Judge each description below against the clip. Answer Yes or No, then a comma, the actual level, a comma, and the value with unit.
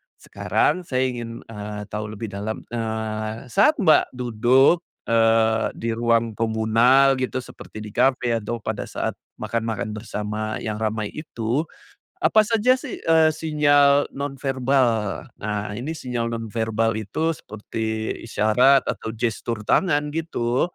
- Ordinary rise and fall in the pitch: Yes, average, 3.7 semitones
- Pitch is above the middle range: No, low, 115 Hz